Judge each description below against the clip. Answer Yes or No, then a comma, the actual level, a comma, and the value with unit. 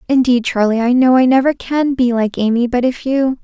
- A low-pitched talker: No, very high, 250 Hz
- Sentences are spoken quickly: Yes, fast, 225 wpm